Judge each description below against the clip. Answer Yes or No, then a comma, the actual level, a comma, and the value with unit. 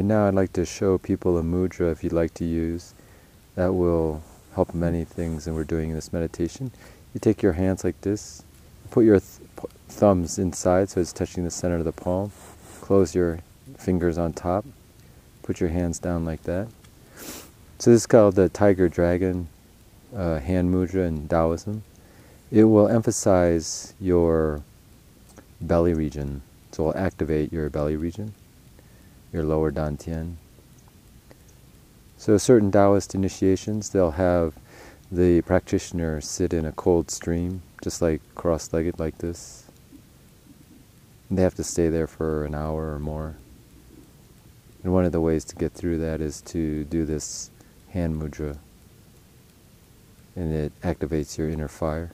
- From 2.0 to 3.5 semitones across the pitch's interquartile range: Yes, average, 2.9 semitones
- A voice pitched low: Yes, very low, 85 Hz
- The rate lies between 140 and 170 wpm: Yes, average, 155 wpm